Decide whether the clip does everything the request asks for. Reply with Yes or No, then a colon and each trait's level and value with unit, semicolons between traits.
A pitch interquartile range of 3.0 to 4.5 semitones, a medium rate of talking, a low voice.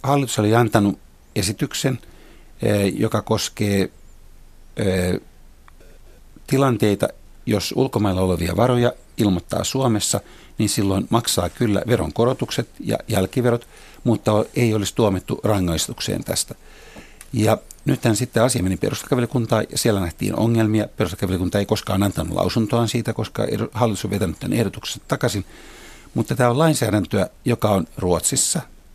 Yes: average, 4.1 semitones; average, 115 wpm; low, 105 Hz